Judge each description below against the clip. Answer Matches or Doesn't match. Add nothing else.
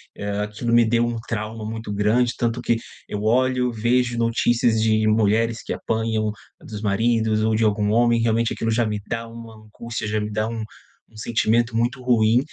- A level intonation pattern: Matches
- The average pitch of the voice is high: Doesn't match